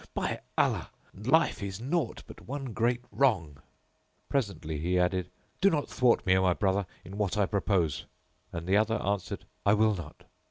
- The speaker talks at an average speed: Yes, average, 170 wpm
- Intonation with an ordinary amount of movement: Yes, average, 4.7 semitones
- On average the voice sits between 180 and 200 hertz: No, low, 100 Hz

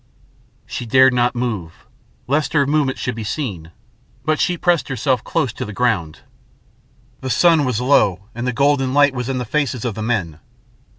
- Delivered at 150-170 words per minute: No, average, 180 wpm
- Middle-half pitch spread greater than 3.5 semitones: Yes, average, 3.9 semitones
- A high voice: No, low, 125 Hz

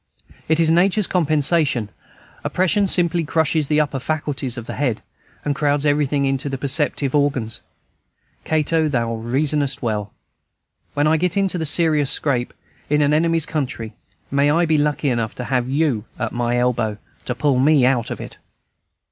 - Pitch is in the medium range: Yes, medium, 145 Hz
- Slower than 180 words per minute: Yes, average, 165 wpm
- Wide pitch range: No, average, 3.8 semitones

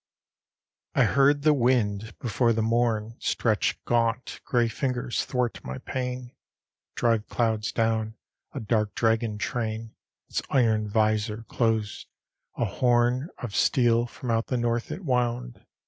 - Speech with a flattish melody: Yes, narrow, 2.0 semitones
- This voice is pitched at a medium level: No, low, 115 Hz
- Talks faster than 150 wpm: No, slow, 135 wpm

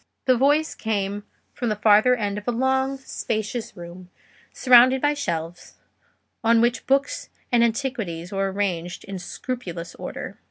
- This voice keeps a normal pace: Yes, average, 145 wpm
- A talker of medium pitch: No, high, 225 Hz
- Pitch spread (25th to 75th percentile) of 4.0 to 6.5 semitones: Yes, average, 4.7 semitones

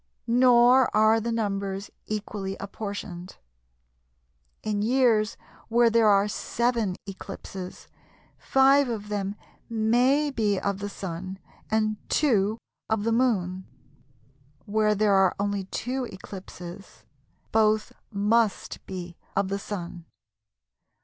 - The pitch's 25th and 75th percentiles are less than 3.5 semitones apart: Yes, average, 2.8 semitones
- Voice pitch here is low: No, high, 210 Hz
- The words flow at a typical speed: No, slow, 110 wpm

